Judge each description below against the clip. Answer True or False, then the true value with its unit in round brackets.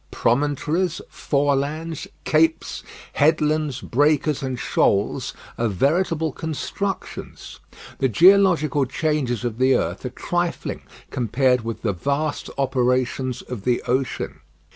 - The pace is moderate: False (105 wpm)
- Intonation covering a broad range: False (3.7 semitones)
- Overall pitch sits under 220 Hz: True (140 Hz)